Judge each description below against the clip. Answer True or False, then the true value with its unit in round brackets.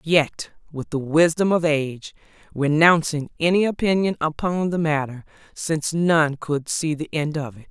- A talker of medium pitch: True (155 Hz)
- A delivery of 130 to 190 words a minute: True (155 wpm)